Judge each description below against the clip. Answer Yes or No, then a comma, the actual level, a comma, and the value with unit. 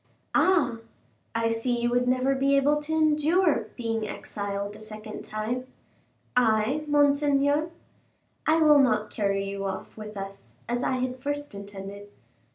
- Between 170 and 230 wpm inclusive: No, average, 145 wpm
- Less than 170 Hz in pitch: No, high, 245 Hz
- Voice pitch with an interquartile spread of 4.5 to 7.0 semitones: Yes, average, 5.2 semitones